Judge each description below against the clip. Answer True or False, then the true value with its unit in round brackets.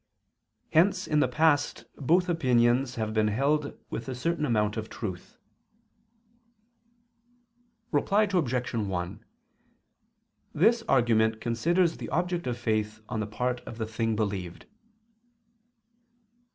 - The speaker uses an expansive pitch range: True (6.3 semitones)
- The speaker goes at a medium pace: False (115 wpm)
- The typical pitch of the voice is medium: False (120 Hz)